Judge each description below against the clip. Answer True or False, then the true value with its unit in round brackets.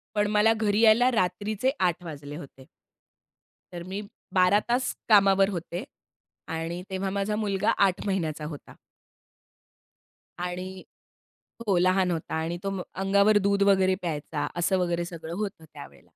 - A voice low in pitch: False (190 Hz)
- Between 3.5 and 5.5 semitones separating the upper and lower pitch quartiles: False (2.9 semitones)